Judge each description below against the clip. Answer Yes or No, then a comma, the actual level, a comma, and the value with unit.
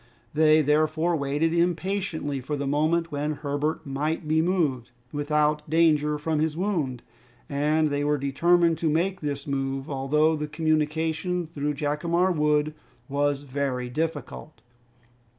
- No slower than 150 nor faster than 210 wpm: No, slow, 135 wpm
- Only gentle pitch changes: Yes, narrow, 2.0 semitones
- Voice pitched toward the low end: No, medium, 150 Hz